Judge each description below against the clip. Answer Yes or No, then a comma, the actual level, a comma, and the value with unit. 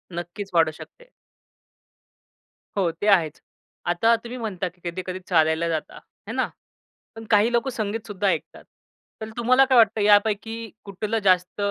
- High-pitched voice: Yes, high, 205 Hz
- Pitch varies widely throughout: No, average, 4.2 semitones